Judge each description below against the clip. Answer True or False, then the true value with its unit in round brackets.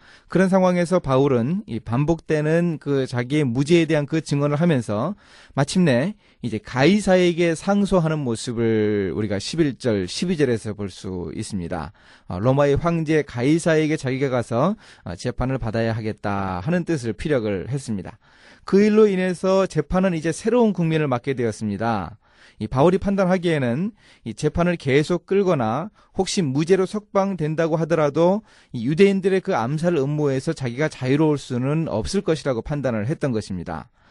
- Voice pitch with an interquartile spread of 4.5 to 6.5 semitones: False (7.0 semitones)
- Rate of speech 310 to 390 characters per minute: True (330 characters per minute)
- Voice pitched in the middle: True (150 Hz)